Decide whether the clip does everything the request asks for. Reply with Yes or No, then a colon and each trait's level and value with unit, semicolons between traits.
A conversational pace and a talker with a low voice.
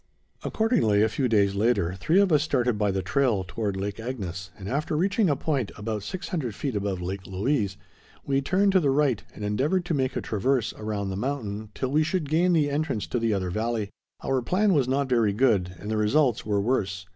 No: fast, 215 wpm; low, 115 Hz